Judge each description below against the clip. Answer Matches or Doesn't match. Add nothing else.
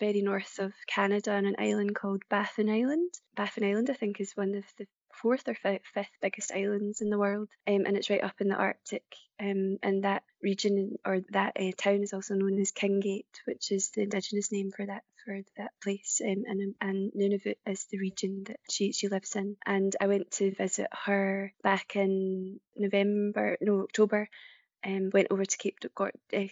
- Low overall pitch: Doesn't match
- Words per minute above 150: Matches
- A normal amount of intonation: Doesn't match